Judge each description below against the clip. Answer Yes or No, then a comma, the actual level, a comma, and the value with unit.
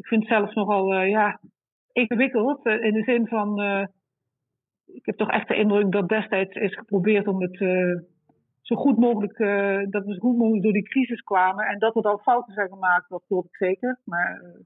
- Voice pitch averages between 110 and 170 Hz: No, high, 205 Hz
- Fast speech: Yes, fast, 220 wpm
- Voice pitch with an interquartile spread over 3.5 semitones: No, average, 2.9 semitones